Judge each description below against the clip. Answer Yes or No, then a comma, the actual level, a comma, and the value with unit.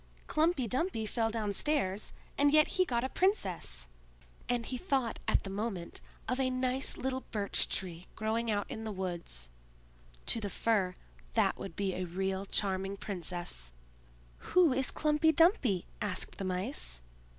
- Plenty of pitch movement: Yes, wide, 5.7 semitones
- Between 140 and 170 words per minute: Yes, average, 150 wpm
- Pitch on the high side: Yes, high, 220 Hz